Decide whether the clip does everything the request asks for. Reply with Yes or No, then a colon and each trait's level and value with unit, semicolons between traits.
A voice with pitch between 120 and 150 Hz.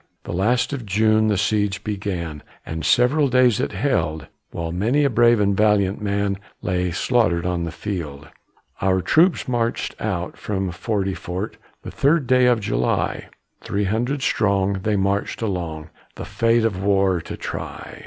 No: low, 100 Hz